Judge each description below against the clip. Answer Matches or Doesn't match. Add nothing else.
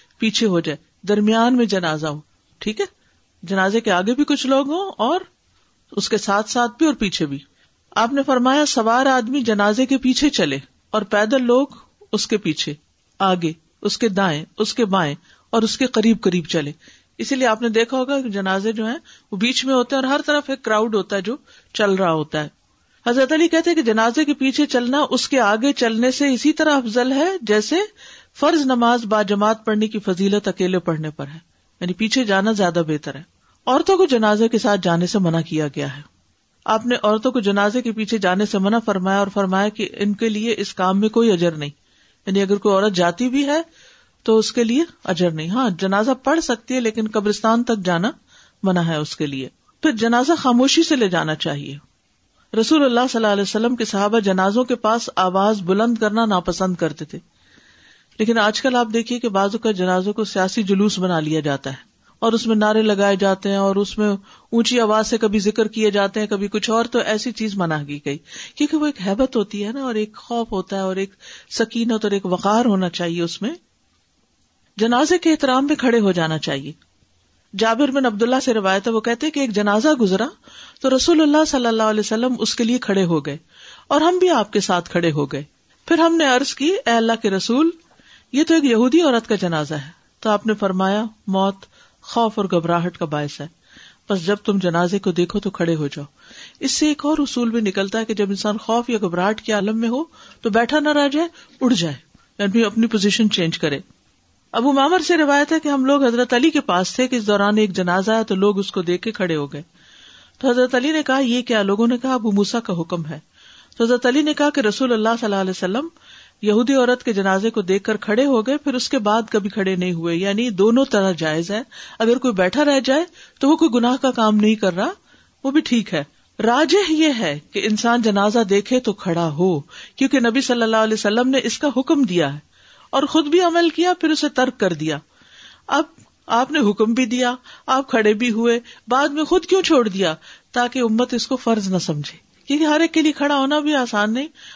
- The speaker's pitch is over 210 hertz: Matches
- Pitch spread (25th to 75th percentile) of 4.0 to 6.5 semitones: Matches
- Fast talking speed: Matches